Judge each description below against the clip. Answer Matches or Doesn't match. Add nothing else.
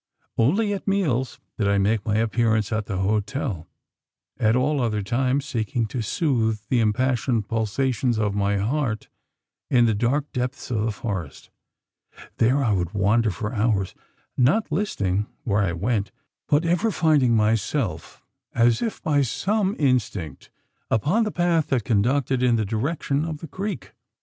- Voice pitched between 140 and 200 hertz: Doesn't match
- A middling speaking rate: Matches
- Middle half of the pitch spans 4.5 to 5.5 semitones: Matches